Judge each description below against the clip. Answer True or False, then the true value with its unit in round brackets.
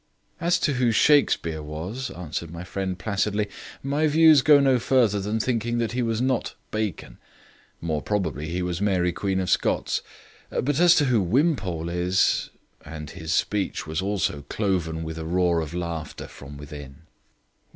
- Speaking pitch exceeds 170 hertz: False (95 Hz)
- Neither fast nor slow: True (165 wpm)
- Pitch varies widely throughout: True (6.7 semitones)